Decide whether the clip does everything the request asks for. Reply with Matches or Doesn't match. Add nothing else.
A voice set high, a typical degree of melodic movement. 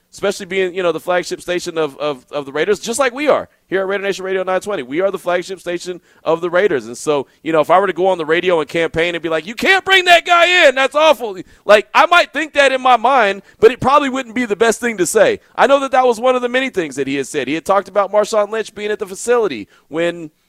Doesn't match